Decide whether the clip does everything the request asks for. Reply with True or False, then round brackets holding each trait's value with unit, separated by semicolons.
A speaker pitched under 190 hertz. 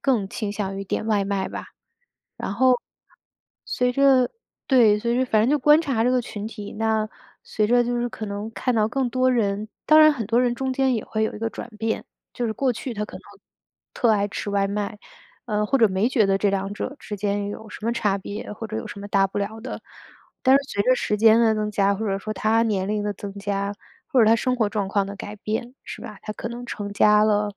False (215 Hz)